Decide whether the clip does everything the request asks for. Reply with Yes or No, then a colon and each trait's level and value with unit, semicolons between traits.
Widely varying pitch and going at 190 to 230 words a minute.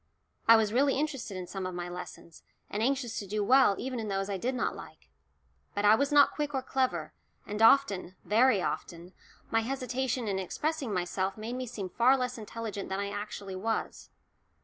No: average, 4.9 semitones; average, 195 wpm